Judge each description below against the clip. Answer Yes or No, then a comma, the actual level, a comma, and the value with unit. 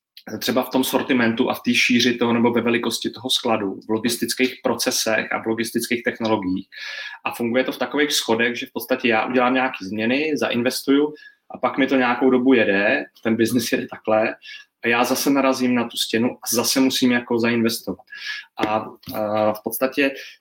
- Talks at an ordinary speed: No, fast, 180 wpm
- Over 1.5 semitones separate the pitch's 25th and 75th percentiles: Yes, narrow, 2.4 semitones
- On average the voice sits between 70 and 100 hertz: No, low, 125 Hz